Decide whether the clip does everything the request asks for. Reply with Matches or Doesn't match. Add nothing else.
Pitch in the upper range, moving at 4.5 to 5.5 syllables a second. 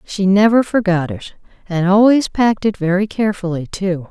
Matches